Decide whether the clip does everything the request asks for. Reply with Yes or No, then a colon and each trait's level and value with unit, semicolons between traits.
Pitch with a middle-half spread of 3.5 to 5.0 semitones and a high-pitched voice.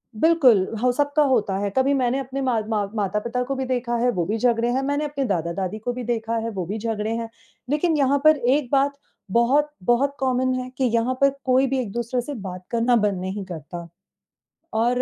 Yes: average, 3.9 semitones; high, 245 Hz